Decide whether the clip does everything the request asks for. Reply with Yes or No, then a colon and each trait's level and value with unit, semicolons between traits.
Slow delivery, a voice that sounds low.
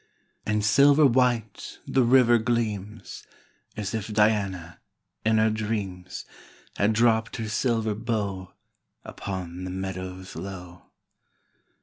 Yes: slow, 115 wpm; low, 105 Hz